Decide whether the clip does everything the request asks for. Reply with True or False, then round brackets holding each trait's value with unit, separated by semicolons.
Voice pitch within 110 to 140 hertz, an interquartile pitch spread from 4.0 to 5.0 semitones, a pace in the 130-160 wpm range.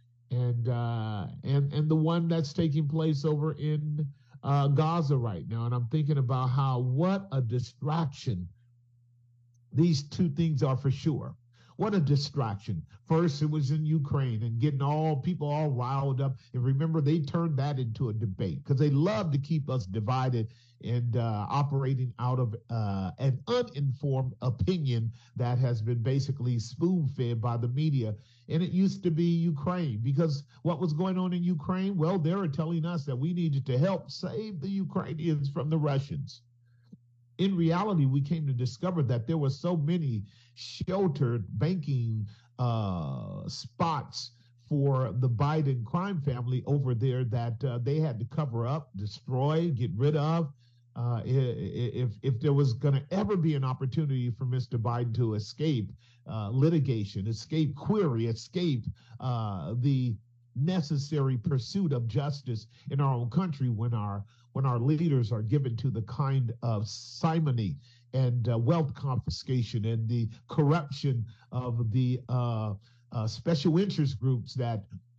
True (135 Hz; 4.4 semitones; 155 wpm)